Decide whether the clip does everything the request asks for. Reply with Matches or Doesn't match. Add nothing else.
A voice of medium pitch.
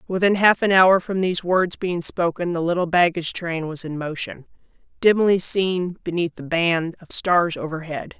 Matches